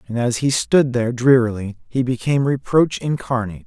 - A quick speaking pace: No, average, 165 wpm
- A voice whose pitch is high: No, low, 125 Hz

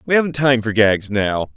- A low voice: Yes, low, 115 Hz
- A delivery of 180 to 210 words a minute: No, fast, 230 wpm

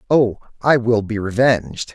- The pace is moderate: Yes, average, 155 wpm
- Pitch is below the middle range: Yes, low, 115 Hz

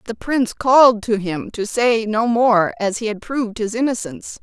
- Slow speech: No, fast, 205 wpm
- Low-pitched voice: No, high, 225 Hz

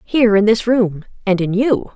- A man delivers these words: No, female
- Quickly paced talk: Yes, fast, 215 wpm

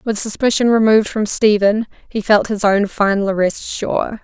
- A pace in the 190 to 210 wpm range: No, average, 170 wpm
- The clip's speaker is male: No, female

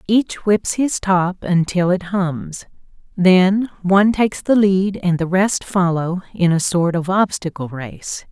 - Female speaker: Yes, female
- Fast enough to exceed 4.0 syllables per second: No, 3.8 syllables/s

